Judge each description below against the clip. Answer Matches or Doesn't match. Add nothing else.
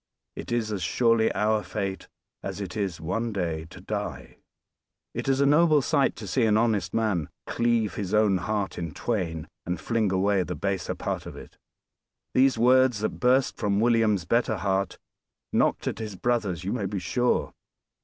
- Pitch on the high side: Doesn't match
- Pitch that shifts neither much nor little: Matches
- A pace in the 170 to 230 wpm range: Matches